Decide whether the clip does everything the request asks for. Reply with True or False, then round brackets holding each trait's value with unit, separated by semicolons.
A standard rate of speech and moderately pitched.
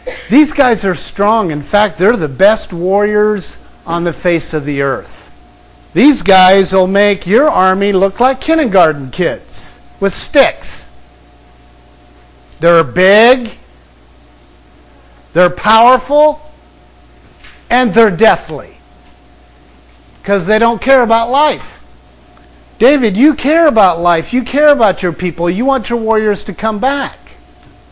False (125 wpm; 180 Hz)